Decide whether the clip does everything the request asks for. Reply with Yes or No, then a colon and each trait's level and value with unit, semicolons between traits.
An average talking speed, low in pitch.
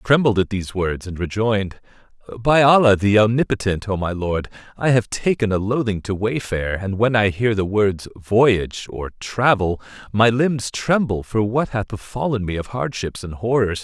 Yes: average, 180 wpm; low, 110 Hz